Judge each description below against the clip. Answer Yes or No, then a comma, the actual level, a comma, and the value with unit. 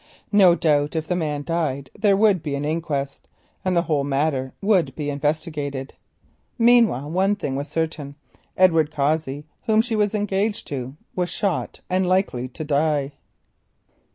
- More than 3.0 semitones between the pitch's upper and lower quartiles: Yes, average, 4.7 semitones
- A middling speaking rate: Yes, average, 155 wpm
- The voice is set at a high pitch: No, medium, 155 Hz